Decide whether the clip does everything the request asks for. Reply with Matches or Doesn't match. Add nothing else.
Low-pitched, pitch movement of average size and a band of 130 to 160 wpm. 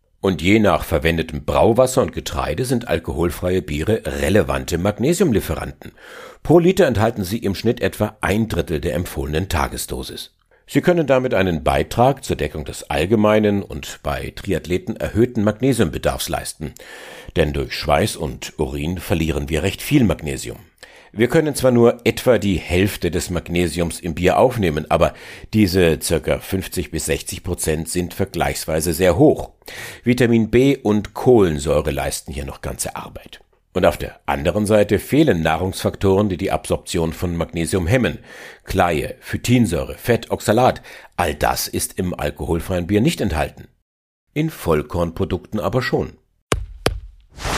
Matches